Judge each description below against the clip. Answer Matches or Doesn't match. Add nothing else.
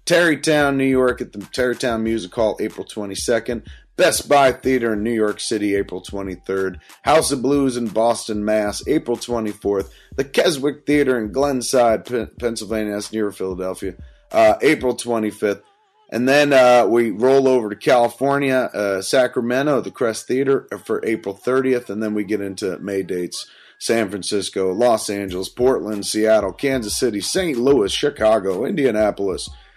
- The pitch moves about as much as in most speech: Matches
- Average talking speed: Matches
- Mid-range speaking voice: Doesn't match